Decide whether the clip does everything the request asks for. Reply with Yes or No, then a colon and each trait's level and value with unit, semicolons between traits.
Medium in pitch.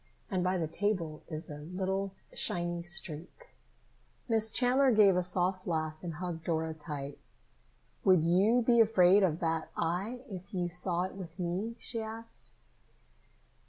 Yes: medium, 180 Hz